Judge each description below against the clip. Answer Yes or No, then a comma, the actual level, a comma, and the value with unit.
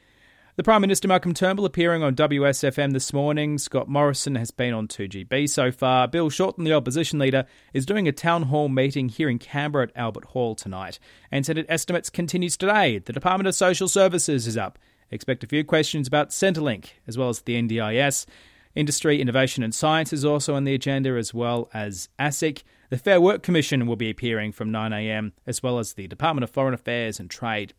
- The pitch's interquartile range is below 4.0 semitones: No, average, 5.0 semitones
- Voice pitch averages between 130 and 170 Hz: Yes, low, 135 Hz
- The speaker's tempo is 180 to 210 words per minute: Yes, average, 195 wpm